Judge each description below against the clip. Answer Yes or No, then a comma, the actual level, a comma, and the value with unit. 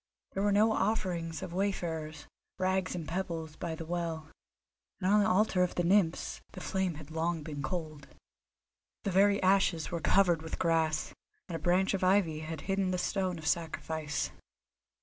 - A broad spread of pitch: No, average, 3.0 semitones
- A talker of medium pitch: Yes, medium, 175 Hz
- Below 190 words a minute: Yes, average, 170 wpm